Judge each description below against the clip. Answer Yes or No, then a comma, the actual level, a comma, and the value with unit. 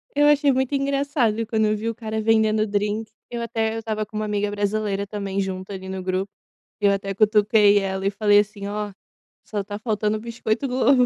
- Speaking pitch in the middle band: No, high, 215 Hz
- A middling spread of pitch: No, narrow, 1.9 semitones